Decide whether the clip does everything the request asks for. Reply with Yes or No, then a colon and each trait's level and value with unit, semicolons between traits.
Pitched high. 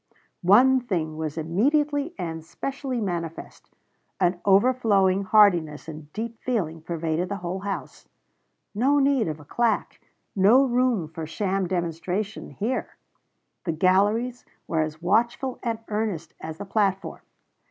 Yes: high, 195 Hz